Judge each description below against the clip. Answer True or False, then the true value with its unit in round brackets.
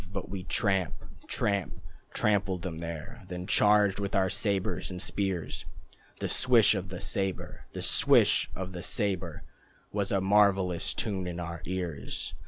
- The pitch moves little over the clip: True (2.0 semitones)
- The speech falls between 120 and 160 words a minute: True (150 wpm)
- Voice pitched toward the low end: True (95 Hz)